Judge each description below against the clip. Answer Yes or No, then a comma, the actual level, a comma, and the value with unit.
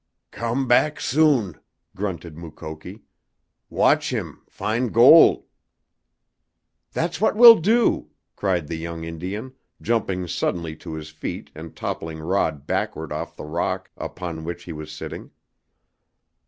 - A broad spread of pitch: Yes, wide, 6.8 semitones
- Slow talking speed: Yes, slow, 125 wpm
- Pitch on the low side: Yes, very low, 90 Hz